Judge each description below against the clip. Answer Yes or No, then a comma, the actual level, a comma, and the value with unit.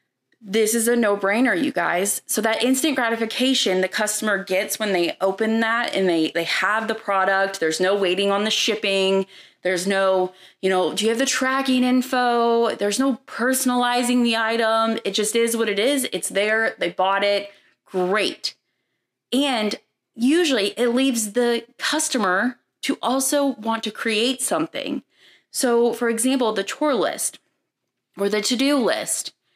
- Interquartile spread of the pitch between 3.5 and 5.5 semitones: Yes, average, 4.2 semitones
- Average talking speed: Yes, average, 160 wpm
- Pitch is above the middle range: Yes, high, 225 Hz